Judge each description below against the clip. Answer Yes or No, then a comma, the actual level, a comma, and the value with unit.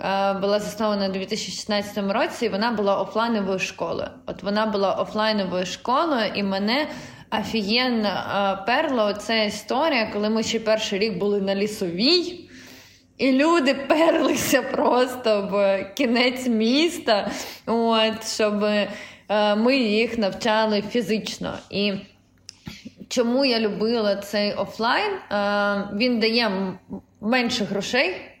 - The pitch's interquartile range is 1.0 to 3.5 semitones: Yes, average, 3.2 semitones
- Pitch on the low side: No, high, 215 Hz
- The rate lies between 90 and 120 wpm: Yes, average, 110 wpm